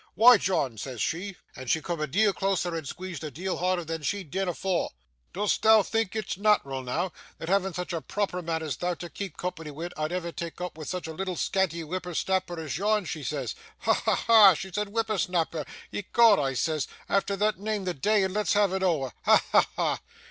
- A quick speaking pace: Yes, fast, 220 wpm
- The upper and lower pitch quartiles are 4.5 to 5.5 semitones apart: No, average, 3.7 semitones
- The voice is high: No, medium, 180 Hz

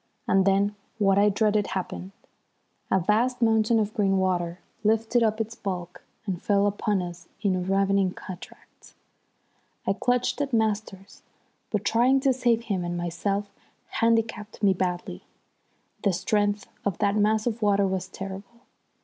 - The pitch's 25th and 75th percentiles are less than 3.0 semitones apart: Yes, narrow, 2.5 semitones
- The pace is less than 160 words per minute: Yes, average, 150 wpm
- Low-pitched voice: No, high, 205 Hz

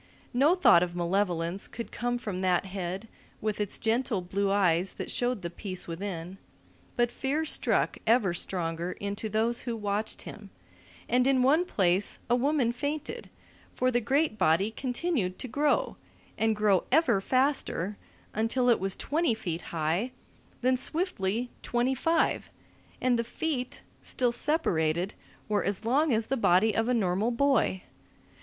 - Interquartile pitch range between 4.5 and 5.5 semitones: Yes, average, 5.2 semitones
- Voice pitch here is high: Yes, high, 220 Hz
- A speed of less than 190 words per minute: Yes, average, 150 wpm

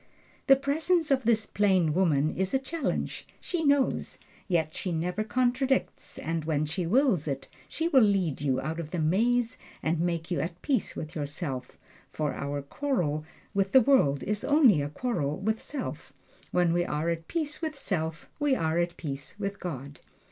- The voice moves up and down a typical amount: No, wide, 8.6 semitones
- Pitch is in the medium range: Yes, medium, 180 Hz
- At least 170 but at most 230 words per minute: Yes, average, 175 wpm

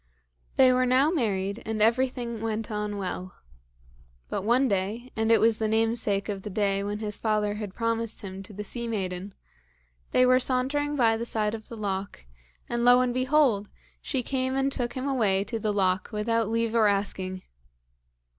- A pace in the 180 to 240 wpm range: Yes, average, 185 wpm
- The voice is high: Yes, high, 225 Hz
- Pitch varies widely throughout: No, average, 3.3 semitones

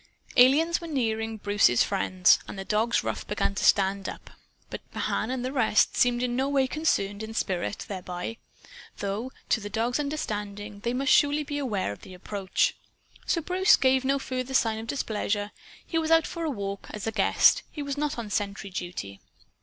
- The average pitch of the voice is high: Yes, high, 225 Hz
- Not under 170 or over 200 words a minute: Yes, average, 190 wpm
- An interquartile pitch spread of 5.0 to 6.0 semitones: Yes, average, 5.3 semitones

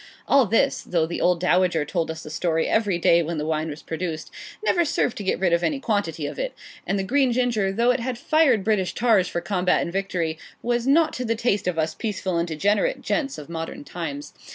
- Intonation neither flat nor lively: No, wide, 6.1 semitones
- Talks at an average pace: No, fast, 225 wpm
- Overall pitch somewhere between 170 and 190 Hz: Yes, medium, 185 Hz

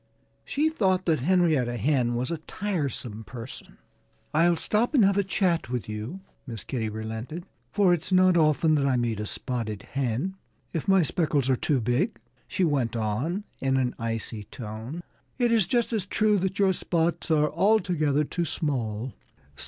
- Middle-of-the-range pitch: Yes, medium, 150 Hz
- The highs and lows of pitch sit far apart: Yes, wide, 7.4 semitones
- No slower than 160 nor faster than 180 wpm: Yes, average, 170 wpm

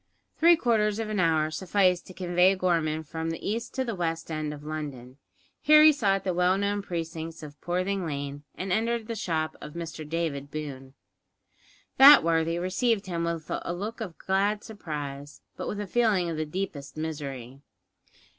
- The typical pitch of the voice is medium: Yes, medium, 170 Hz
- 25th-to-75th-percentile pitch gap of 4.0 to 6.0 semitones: Yes, average, 4.6 semitones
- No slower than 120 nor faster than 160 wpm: No, average, 175 wpm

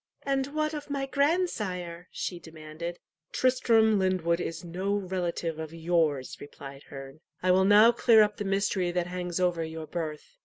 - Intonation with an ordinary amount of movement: Yes, average, 4.6 semitones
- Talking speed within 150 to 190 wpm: Yes, average, 160 wpm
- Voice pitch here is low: No, medium, 180 Hz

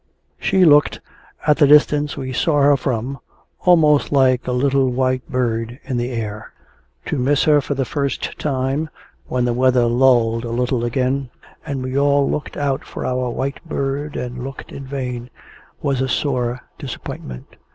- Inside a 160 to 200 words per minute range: Yes, average, 165 wpm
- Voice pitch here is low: Yes, low, 130 Hz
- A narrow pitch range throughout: Yes, narrow, 2.3 semitones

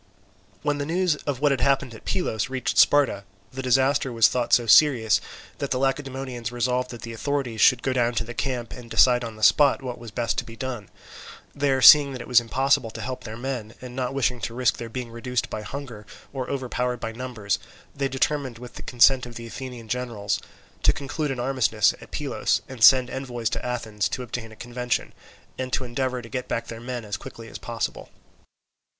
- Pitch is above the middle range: No, low, 125 Hz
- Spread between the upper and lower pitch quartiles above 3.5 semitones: No, narrow, 2.4 semitones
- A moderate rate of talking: No, fast, 210 wpm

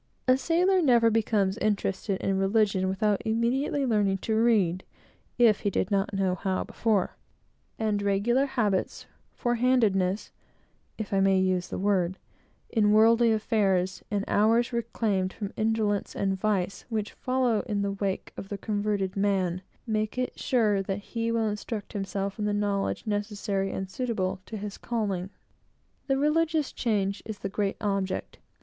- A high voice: Yes, high, 205 Hz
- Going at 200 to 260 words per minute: No, average, 150 wpm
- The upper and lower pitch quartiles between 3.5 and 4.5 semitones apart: No, average, 2.7 semitones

